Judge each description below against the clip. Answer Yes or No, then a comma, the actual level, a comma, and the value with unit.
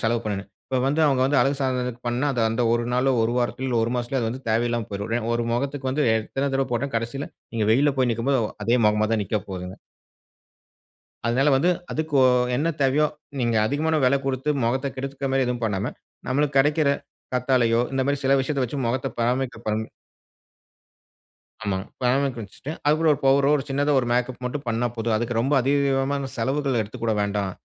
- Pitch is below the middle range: Yes, low, 130 Hz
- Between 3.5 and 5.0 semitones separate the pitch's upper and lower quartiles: No, average, 3.0 semitones